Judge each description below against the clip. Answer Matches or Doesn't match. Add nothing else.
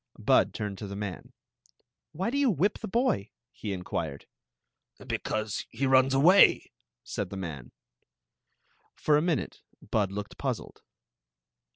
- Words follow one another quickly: Doesn't match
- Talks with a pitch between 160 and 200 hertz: Doesn't match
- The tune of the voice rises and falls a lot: Matches